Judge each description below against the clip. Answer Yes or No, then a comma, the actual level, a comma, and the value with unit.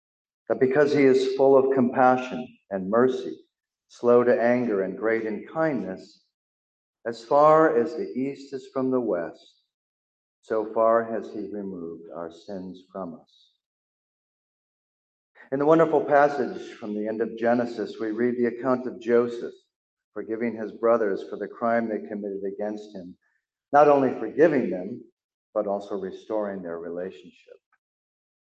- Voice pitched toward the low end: Yes, low, 115 Hz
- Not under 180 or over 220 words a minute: No, average, 145 wpm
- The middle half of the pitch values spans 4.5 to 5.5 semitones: Yes, average, 4.8 semitones